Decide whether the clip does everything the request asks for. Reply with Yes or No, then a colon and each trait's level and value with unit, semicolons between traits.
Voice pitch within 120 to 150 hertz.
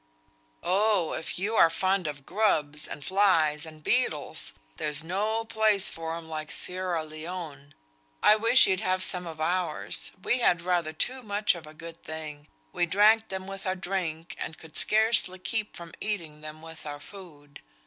No: medium, 175 Hz